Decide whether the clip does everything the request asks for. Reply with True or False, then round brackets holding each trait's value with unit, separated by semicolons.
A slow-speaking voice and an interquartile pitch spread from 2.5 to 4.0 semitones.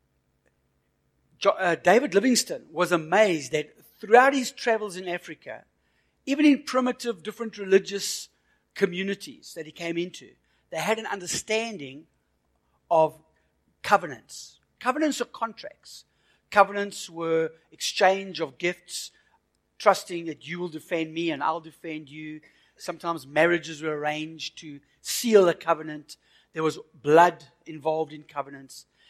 False (120 wpm; 4.8 semitones)